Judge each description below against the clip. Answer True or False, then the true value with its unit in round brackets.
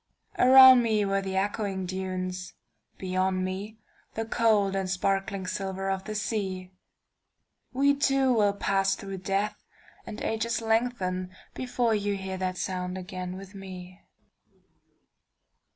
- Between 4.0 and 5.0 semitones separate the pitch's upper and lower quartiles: False (2.7 semitones)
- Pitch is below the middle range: False (195 Hz)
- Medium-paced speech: False (115 wpm)